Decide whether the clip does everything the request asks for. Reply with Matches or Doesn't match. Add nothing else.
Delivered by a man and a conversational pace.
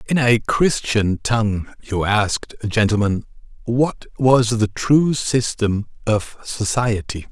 Doesn't match